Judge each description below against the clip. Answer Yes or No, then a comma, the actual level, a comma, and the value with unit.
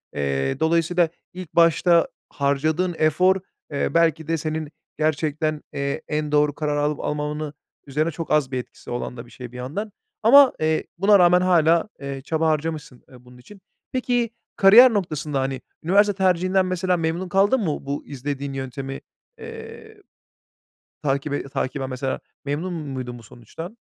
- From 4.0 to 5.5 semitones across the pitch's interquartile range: Yes, average, 4.5 semitones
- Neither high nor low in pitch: Yes, medium, 155 Hz